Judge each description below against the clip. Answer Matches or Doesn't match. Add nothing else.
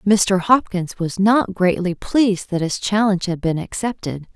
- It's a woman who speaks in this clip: Matches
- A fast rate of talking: Doesn't match